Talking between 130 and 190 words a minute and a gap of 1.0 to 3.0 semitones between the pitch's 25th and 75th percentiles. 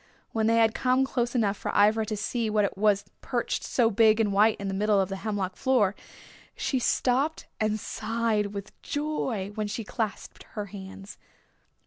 Yes: average, 180 wpm; narrow, 2.4 semitones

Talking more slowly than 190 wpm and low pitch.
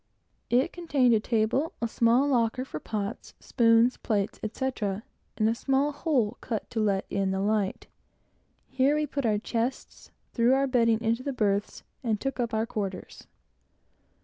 No: average, 160 wpm; high, 230 Hz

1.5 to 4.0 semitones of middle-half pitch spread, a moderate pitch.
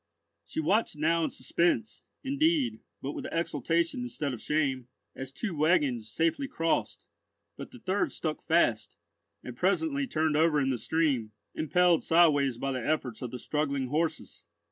No: average, 4.5 semitones; medium, 155 Hz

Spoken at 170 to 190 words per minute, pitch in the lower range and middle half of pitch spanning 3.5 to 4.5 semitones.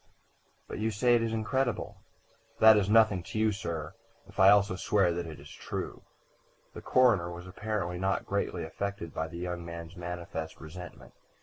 Yes: average, 175 wpm; very low, 95 Hz; average, 4.0 semitones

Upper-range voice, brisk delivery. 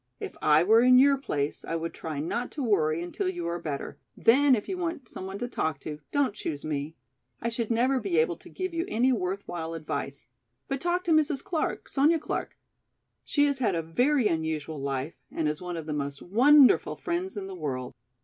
Yes: high, 200 Hz; fast, 210 wpm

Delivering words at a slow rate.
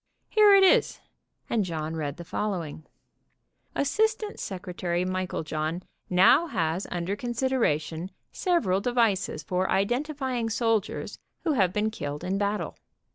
Yes: slow, 120 wpm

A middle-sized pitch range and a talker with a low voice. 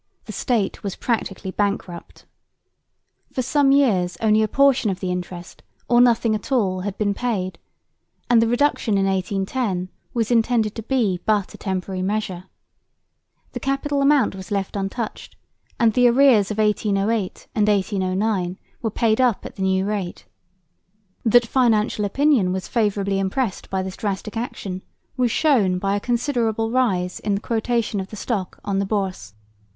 No: average, 3.7 semitones; high, 210 Hz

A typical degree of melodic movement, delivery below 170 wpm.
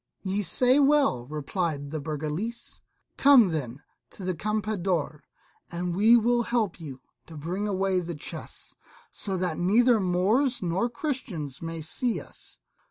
No: wide, 6.4 semitones; average, 140 wpm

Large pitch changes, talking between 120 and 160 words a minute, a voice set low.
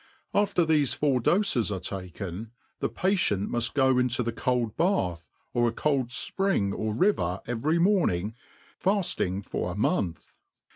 Yes: wide, 8.8 semitones; average, 150 wpm; low, 120 Hz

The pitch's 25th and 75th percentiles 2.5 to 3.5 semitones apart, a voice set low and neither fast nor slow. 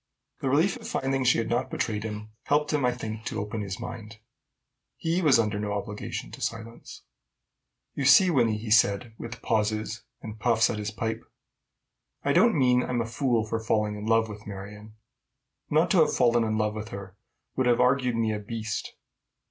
Yes: average, 2.8 semitones; low, 115 Hz; average, 190 wpm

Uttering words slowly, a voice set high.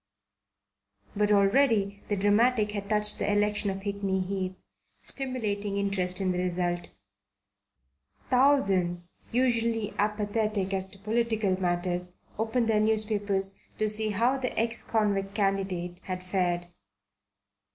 Yes: slow, 120 wpm; high, 205 Hz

